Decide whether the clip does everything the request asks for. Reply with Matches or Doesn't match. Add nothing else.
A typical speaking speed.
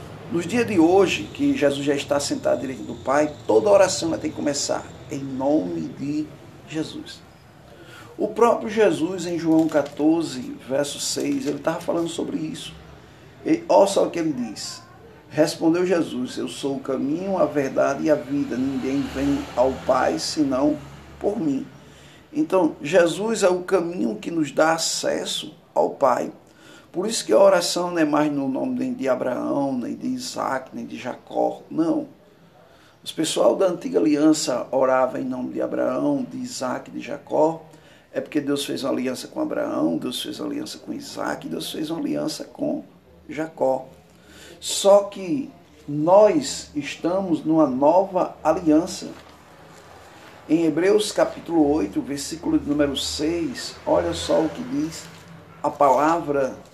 Matches